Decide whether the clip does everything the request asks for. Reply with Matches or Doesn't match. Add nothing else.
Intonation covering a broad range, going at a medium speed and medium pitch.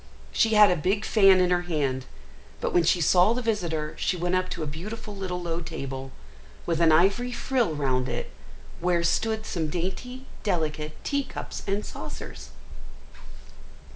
Doesn't match